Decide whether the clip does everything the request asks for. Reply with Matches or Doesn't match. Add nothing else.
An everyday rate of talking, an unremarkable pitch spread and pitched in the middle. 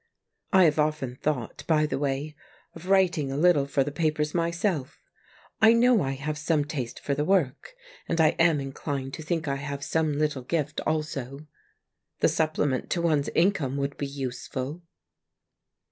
Matches